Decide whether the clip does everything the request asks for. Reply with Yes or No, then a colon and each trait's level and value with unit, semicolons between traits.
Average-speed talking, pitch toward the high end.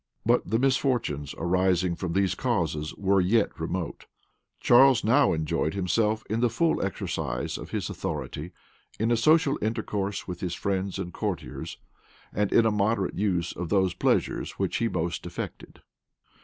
No: average, 155 wpm; low, 100 Hz